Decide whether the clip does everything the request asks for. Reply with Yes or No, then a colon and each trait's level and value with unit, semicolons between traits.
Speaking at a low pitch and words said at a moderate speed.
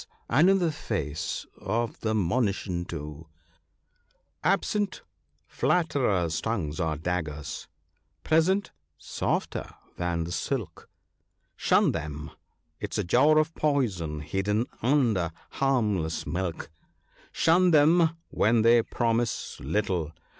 No: low, 105 Hz; slow, 110 wpm